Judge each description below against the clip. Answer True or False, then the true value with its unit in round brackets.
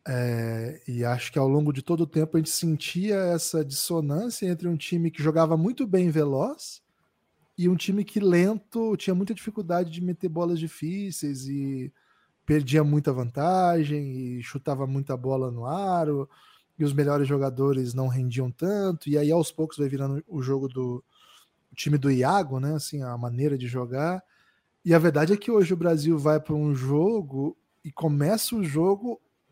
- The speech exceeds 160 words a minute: True (175 wpm)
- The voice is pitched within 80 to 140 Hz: False (155 Hz)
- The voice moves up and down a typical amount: True (4.5 semitones)